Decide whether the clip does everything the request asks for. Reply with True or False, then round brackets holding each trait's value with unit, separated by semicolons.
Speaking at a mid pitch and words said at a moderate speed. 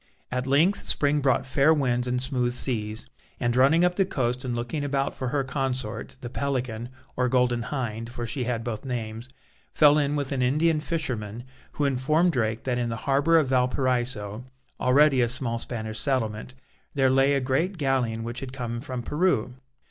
False (130 Hz; 180 wpm)